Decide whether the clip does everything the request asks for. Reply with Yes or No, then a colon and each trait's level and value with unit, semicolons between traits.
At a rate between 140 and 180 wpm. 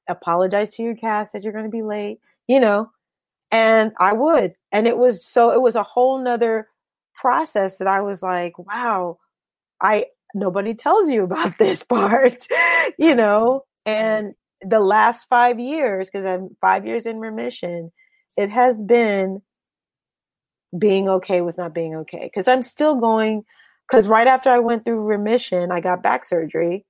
Yes: average, 165 wpm